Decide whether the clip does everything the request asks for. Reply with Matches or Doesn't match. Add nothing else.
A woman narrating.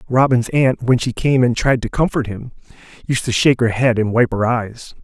Doesn't match